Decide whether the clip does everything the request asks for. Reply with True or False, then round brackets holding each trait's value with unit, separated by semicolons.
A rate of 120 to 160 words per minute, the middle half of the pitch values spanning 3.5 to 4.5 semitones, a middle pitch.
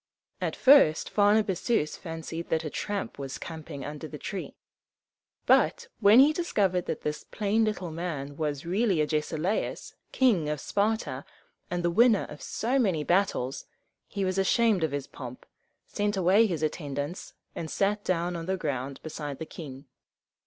False (155 wpm; 5.3 semitones; 175 Hz)